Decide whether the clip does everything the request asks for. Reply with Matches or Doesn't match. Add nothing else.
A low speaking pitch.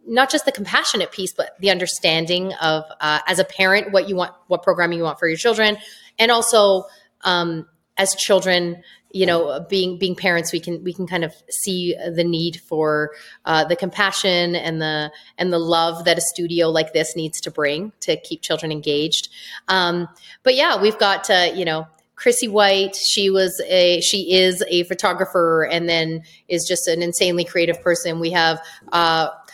Doesn't match